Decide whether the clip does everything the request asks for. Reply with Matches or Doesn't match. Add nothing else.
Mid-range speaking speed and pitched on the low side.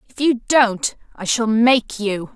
Doesn't match